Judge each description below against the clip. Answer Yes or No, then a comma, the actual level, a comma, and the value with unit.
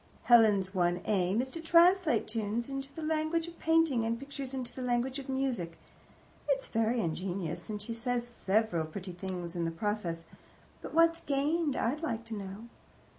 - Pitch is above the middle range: Yes, high, 235 Hz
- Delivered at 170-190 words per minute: Yes, average, 175 wpm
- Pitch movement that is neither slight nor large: No, wide, 6.3 semitones